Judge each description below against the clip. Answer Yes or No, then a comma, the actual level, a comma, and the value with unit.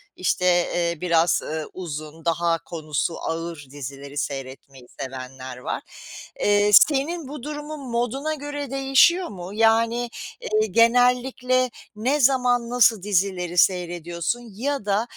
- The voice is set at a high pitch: Yes, high, 205 Hz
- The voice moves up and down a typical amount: No, wide, 7.4 semitones